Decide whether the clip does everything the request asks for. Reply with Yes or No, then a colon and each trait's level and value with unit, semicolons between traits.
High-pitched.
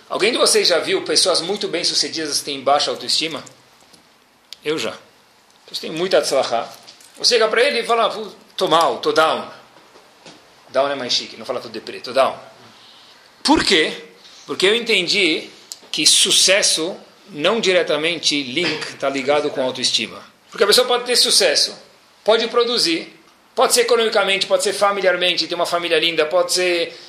No: medium, 180 Hz